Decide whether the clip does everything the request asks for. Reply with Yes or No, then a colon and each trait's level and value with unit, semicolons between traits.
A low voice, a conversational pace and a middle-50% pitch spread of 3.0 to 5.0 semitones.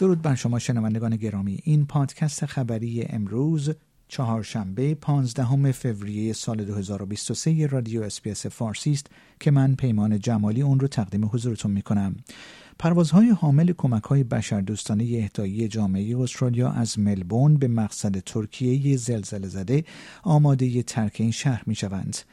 Yes: low, 120 Hz; average, 130 wpm; average, 4.6 semitones